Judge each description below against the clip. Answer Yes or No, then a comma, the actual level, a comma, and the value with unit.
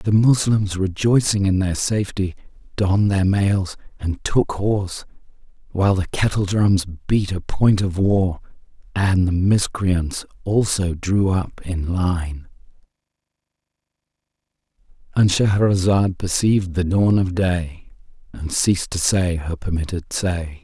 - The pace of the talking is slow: Yes, slow, 120 wpm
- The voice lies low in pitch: Yes, very low, 95 Hz